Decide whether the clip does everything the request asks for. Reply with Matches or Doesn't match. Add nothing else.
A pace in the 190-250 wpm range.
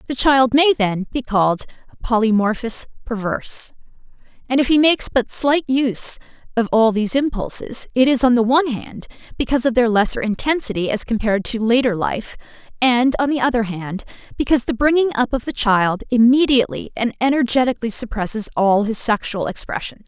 Doesn't match